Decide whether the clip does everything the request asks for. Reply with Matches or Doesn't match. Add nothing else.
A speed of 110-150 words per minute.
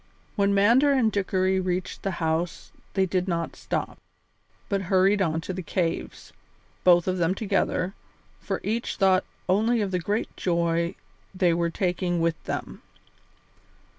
Matches